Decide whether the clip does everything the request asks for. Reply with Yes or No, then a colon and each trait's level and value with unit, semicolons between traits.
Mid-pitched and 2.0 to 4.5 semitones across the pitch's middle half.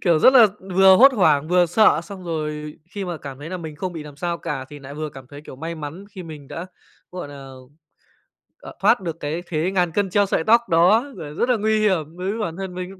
Yes: medium, 170 Hz; average, 4.1 semitones